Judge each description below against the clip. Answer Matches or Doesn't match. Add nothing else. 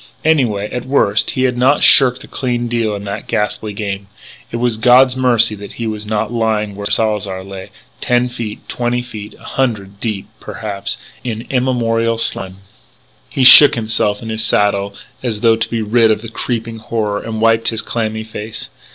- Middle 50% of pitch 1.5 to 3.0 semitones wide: Matches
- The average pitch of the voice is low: Matches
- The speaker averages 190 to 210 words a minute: Doesn't match